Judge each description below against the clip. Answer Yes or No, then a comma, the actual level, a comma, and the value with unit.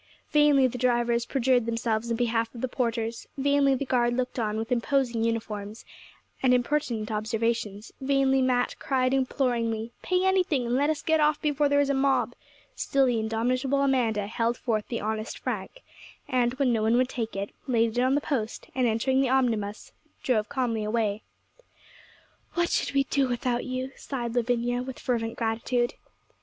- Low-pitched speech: No, high, 245 Hz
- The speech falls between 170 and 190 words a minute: Yes, average, 175 wpm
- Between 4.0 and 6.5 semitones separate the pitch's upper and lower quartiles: No, average, 2.8 semitones